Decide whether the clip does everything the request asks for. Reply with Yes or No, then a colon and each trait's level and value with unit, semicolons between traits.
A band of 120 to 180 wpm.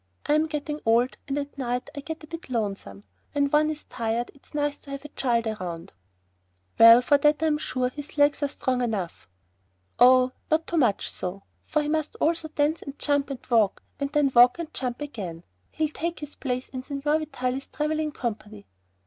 No: average, 190 wpm